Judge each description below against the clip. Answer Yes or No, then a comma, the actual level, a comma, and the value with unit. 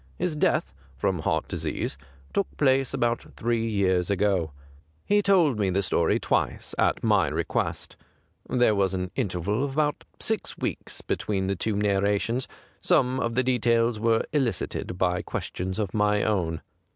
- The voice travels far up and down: No, average, 4.9 semitones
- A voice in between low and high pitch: No, low, 105 Hz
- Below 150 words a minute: No, average, 155 wpm